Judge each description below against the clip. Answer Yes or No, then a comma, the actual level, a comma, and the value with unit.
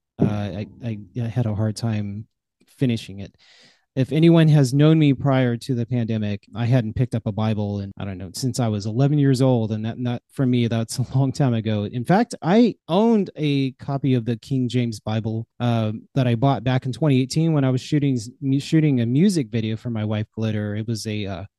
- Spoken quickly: Yes, fast, 220 wpm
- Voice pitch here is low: Yes, low, 120 Hz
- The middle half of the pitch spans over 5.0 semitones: No, average, 3.8 semitones